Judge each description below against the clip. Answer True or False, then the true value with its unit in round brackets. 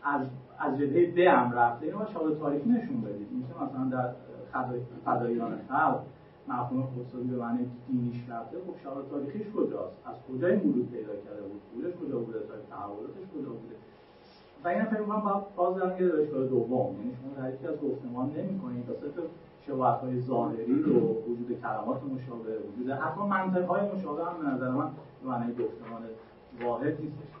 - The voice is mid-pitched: False (130 Hz)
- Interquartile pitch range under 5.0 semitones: False (5.6 semitones)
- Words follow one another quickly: True (175 wpm)